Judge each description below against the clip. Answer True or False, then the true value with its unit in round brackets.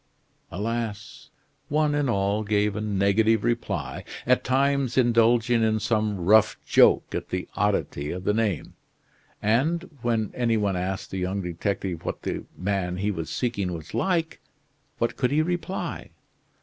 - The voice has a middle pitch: False (110 Hz)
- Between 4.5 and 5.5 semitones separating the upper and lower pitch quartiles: False (3.7 semitones)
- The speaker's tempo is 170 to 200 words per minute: False (150 wpm)